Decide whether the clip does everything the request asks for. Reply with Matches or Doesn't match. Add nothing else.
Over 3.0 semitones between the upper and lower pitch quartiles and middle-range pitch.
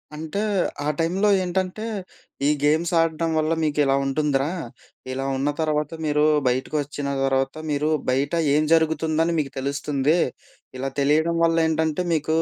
Doesn't match